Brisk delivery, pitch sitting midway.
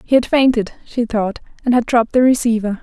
No: fast, 210 wpm; high, 235 Hz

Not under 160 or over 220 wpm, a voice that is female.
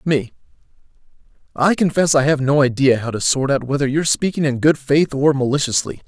No: average, 190 wpm; male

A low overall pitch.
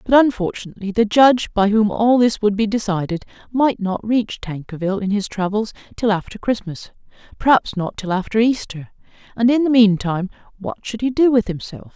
No: high, 215 Hz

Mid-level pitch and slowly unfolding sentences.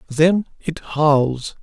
Yes: medium, 155 Hz; slow, 110 wpm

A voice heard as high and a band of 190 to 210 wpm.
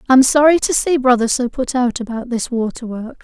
No: very high, 250 Hz; fast, 225 wpm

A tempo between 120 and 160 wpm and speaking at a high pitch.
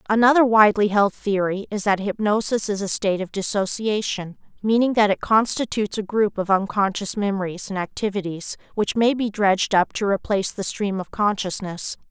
No: average, 170 wpm; high, 205 Hz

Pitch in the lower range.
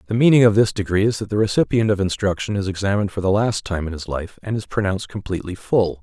Yes: low, 100 Hz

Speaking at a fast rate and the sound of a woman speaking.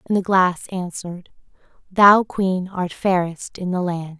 No: average, 155 wpm; female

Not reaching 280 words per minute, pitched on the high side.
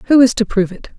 No: fast, 305 wpm; high, 225 Hz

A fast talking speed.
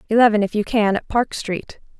Yes: fast, 210 wpm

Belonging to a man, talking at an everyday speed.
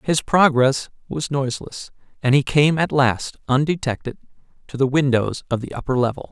Yes: male; average, 160 wpm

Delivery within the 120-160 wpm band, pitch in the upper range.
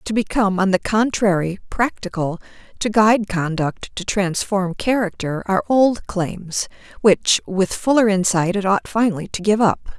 Yes: average, 150 wpm; high, 200 Hz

